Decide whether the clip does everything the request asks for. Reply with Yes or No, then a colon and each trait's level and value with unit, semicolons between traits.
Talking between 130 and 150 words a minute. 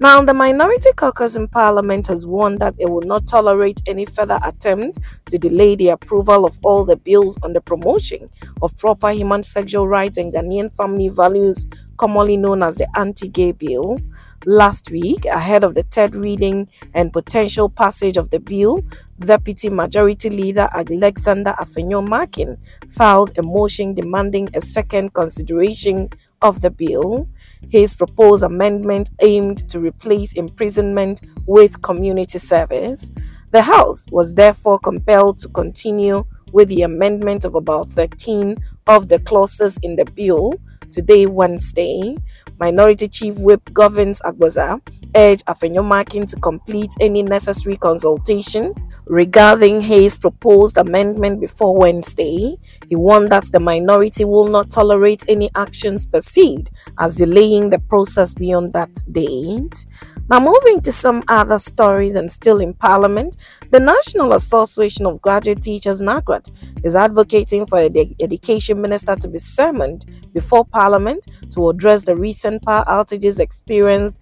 Yes: average, 140 wpm